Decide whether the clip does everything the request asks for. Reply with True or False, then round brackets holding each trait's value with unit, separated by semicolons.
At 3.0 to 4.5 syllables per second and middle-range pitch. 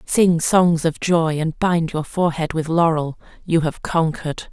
True (4.4 syllables/s; 165 Hz)